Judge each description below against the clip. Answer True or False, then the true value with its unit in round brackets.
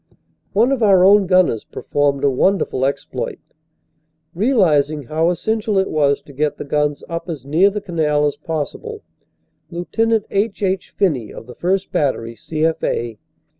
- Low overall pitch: False (165 Hz)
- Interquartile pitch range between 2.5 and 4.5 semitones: False (5.4 semitones)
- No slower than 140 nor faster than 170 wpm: True (155 wpm)